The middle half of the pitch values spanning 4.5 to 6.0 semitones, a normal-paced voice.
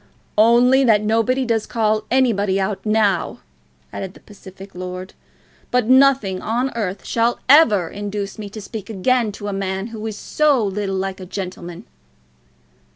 No: average, 3.3 semitones; average, 160 wpm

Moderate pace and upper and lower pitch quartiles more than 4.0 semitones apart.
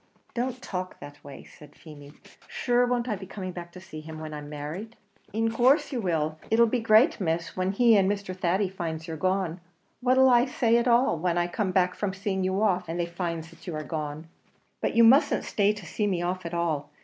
No: fast, 230 wpm; average, 5.2 semitones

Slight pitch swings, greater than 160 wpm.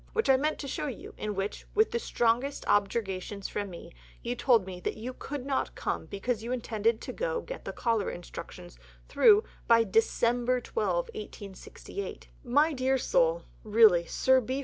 No: average, 5.1 semitones; average, 170 wpm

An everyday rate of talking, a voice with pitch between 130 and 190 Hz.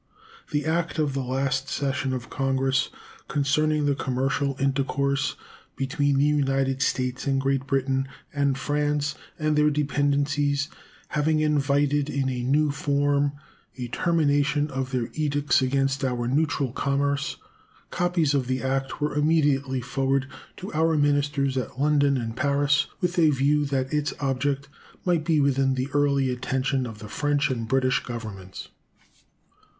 Yes: average, 145 wpm; medium, 140 Hz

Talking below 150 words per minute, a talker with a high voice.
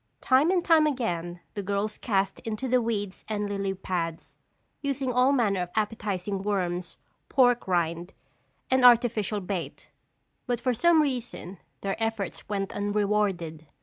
Yes: average, 140 wpm; high, 210 Hz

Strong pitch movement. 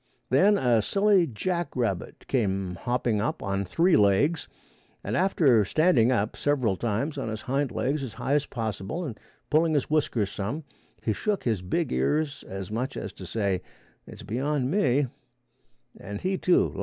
Yes: wide, 6.8 semitones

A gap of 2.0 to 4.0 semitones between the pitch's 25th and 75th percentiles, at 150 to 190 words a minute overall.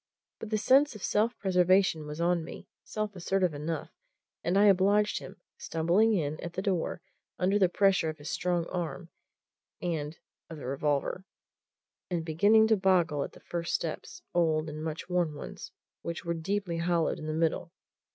Yes: average, 3.4 semitones; average, 170 wpm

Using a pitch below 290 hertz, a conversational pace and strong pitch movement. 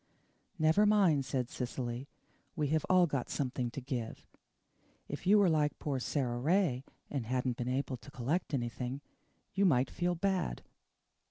No: medium, 140 Hz; average, 155 wpm; average, 5.0 semitones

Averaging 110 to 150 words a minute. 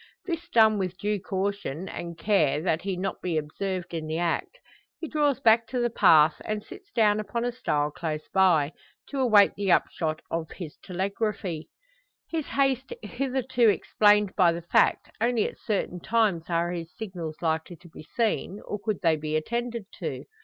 No: average, 175 wpm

